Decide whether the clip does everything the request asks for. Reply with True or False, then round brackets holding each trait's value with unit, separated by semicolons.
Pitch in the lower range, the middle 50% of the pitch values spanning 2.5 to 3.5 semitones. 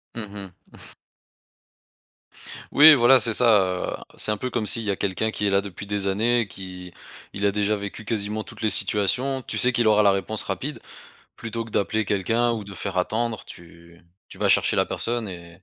True (105 Hz; 2.9 semitones)